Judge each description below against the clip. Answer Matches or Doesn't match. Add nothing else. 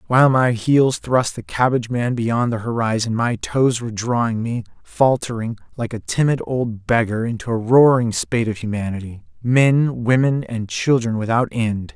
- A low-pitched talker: Matches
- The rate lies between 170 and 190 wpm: Doesn't match